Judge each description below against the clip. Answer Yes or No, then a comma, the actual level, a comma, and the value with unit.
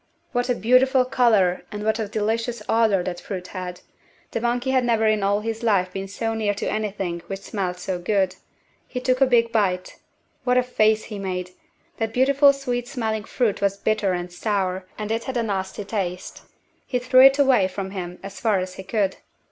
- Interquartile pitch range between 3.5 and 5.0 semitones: Yes, average, 4.1 semitones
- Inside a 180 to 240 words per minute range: Yes, average, 200 wpm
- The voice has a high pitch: Yes, high, 215 Hz